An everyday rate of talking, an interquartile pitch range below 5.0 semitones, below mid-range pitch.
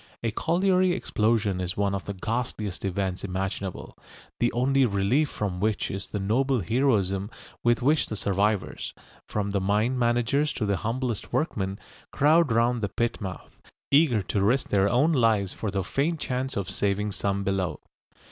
Yes: average, 165 wpm; average, 4.5 semitones; low, 105 Hz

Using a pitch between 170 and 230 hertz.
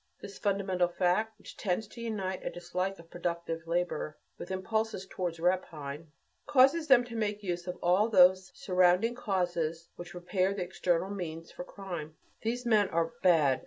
Yes: medium, 185 Hz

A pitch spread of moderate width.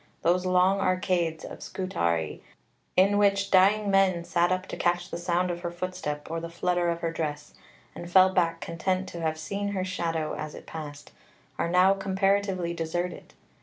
No: narrow, 2.1 semitones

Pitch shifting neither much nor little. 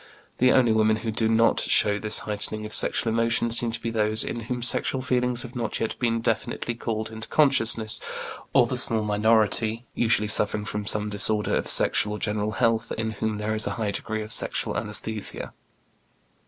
No: narrow, 1.4 semitones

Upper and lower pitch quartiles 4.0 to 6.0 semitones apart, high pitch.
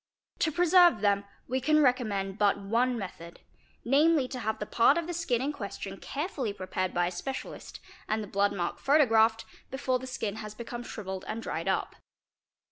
Yes: average, 5.2 semitones; high, 230 Hz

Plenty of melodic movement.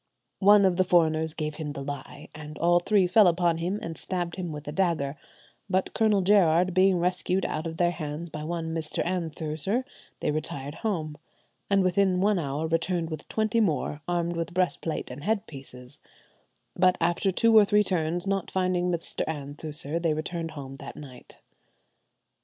No: average, 3.2 semitones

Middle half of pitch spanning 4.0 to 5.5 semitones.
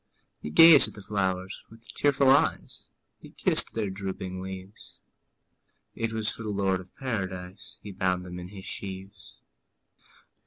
No: average, 3.0 semitones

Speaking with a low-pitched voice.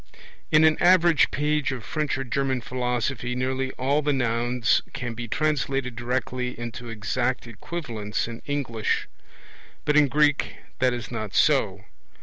Yes: low, 125 Hz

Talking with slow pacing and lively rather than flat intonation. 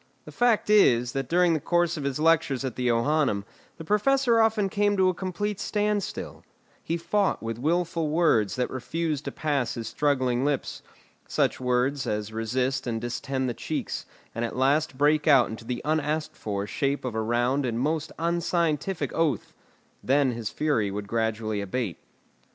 No: average, 170 wpm; wide, 5.7 semitones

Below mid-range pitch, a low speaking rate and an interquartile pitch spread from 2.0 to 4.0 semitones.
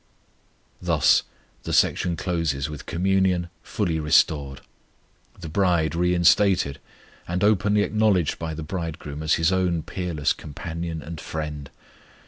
Yes: very low, 85 Hz; slow, 115 wpm; average, 3.0 semitones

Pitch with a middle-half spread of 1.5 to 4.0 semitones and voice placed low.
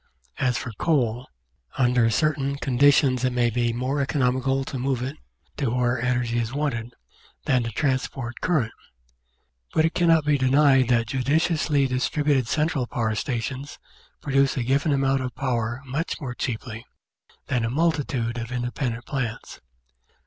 Yes: average, 2.7 semitones; low, 130 Hz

